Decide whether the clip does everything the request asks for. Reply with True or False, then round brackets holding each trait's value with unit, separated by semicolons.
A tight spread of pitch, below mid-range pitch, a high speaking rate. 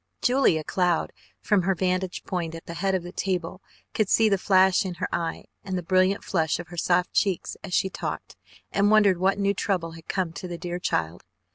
False (2.1 semitones; 185 Hz; 215 wpm)